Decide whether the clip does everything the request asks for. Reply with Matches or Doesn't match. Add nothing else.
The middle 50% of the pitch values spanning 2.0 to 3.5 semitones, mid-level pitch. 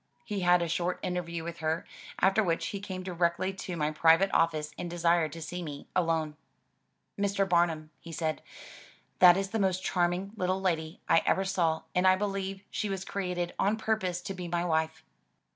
Matches